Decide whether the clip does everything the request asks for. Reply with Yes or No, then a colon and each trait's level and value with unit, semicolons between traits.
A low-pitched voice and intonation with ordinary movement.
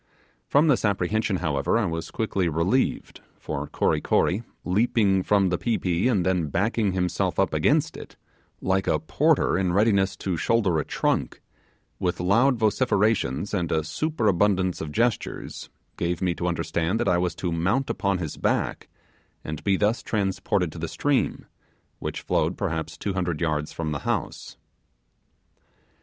Yes: very low, 95 Hz; average, 3.9 semitones